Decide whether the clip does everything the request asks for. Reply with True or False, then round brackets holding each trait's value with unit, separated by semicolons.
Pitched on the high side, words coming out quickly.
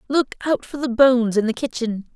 True (245 Hz; 225 wpm)